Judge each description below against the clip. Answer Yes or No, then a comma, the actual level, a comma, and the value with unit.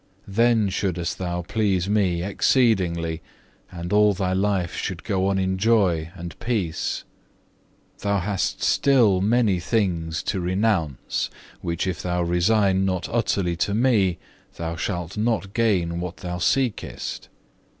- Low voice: Yes, very low, 95 Hz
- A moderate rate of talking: No, slow, 130 wpm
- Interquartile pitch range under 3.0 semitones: No, average, 3.3 semitones